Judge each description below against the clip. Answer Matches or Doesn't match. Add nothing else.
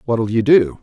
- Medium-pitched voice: Doesn't match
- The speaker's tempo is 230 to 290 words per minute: Doesn't match